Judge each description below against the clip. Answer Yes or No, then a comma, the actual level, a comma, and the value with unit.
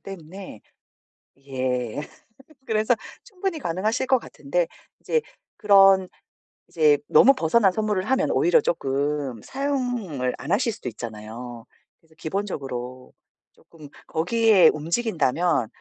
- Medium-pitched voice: Yes, medium, 175 Hz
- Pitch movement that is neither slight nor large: No, wide, 8.7 semitones